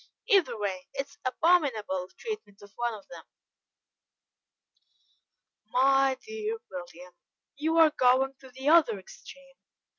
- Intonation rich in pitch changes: Yes, wide, 7.1 semitones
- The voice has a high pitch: Yes, very high, 265 Hz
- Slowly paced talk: Yes, slow, 120 wpm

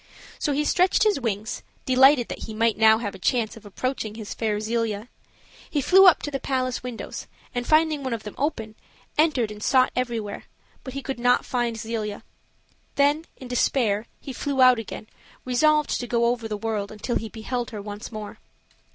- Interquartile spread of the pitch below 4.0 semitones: Yes, average, 3.6 semitones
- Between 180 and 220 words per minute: Yes, average, 190 wpm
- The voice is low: No, high, 240 Hz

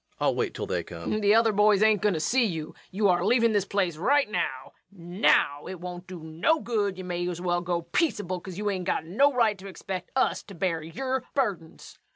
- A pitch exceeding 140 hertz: Yes, high, 190 Hz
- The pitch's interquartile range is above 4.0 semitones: No, average, 3.6 semitones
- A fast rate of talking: Yes, fast, 225 wpm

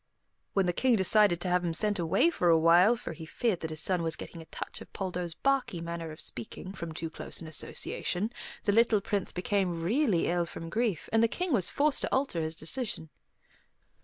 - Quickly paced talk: Yes, fast, 215 wpm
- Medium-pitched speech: Yes, medium, 180 Hz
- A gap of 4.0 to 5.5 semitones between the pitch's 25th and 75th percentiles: Yes, average, 4.9 semitones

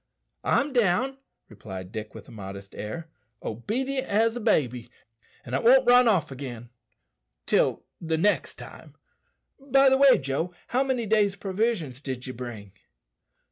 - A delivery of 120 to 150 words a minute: Yes, average, 140 wpm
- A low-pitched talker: No, medium, 175 Hz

